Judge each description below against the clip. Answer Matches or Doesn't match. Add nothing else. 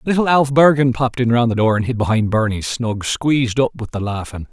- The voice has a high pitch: Doesn't match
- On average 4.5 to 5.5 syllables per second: Doesn't match